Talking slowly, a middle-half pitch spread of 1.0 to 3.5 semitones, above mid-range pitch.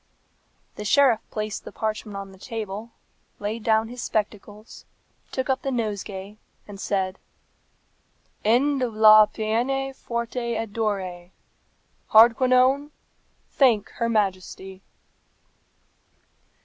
Yes: slow, 110 wpm; average, 2.7 semitones; high, 220 Hz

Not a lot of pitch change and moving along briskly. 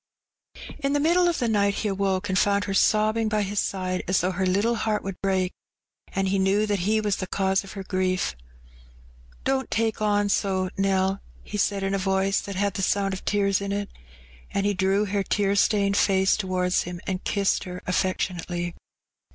Yes: narrow, 1.6 semitones; fast, 210 wpm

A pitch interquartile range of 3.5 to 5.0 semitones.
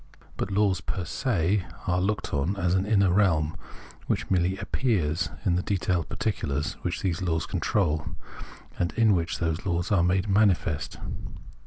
No: average, 3.1 semitones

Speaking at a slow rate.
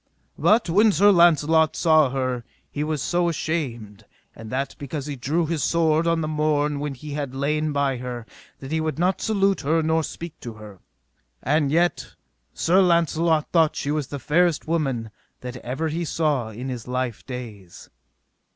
No: average, 175 wpm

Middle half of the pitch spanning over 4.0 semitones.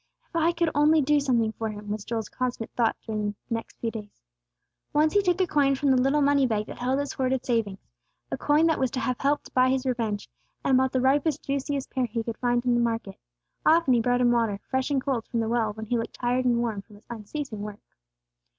No: average, 3.5 semitones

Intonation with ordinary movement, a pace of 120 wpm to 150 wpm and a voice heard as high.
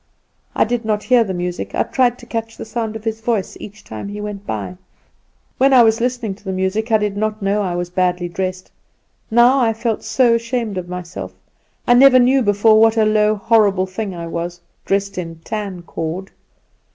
No: average, 3.5 semitones; average, 200 wpm; high, 210 Hz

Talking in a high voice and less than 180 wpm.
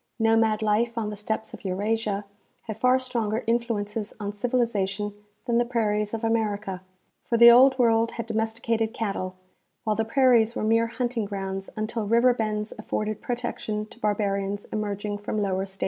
Yes: high, 220 Hz; average, 160 wpm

